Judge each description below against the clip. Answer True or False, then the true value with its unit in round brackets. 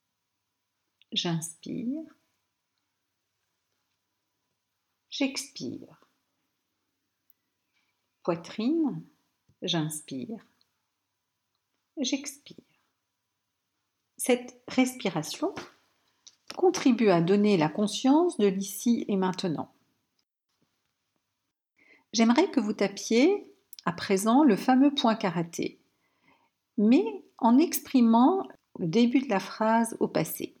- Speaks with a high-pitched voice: True (230 Hz)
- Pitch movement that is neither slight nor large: False (6.4 semitones)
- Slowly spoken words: True (70 wpm)